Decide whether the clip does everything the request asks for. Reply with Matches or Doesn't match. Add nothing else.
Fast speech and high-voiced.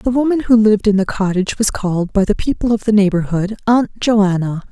Matches